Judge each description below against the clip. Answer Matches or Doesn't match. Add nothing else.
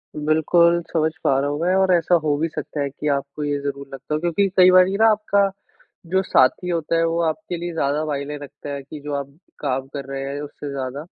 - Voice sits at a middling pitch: Matches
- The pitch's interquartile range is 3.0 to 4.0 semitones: Matches